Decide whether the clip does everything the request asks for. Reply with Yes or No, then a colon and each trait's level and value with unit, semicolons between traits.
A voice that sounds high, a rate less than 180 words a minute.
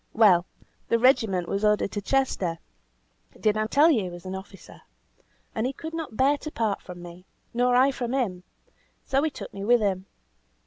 No: high, 220 Hz; average, 190 wpm